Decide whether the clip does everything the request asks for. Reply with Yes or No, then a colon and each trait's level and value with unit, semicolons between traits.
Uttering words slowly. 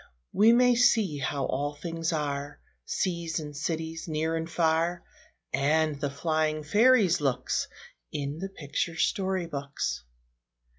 Yes: slow, 130 wpm